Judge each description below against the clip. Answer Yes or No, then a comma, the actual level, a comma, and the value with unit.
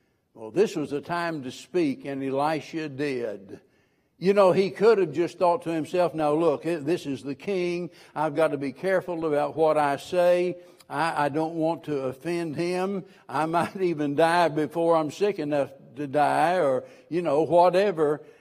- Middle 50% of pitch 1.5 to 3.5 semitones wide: Yes, average, 3.1 semitones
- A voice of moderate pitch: Yes, medium, 165 Hz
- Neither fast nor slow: Yes, average, 180 wpm